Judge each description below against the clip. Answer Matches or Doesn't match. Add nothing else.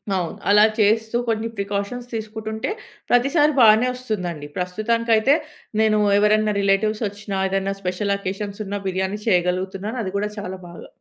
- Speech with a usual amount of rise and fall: Doesn't match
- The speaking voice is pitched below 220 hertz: Matches